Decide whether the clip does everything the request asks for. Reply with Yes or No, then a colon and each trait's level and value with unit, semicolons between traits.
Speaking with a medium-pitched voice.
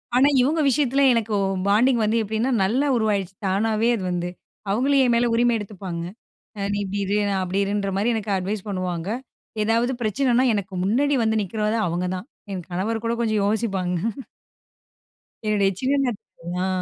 No: high, 215 Hz